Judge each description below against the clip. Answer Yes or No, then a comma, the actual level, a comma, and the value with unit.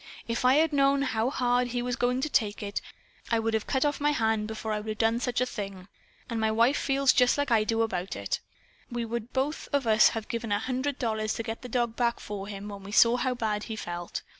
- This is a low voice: No, high, 230 Hz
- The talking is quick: Yes, fast, 255 wpm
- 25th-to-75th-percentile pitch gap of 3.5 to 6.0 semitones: No, average, 2.7 semitones